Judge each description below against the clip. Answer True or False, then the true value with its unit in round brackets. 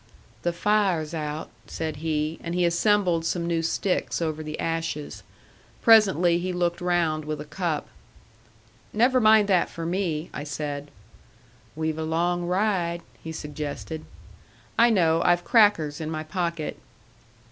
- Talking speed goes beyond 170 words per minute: False (140 wpm)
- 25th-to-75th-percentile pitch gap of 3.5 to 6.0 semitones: False (2.5 semitones)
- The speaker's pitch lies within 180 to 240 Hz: False (170 Hz)